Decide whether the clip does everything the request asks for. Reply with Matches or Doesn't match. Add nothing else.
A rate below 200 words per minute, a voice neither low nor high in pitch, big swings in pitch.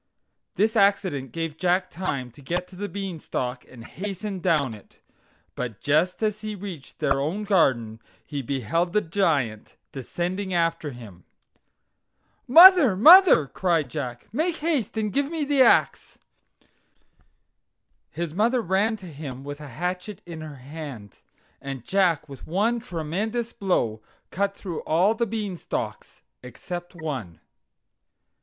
Matches